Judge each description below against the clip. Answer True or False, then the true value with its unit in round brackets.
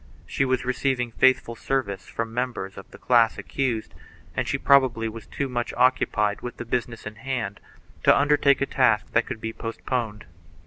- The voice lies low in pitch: True (120 Hz)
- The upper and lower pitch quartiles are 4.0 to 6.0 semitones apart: False (2.6 semitones)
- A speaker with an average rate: True (175 wpm)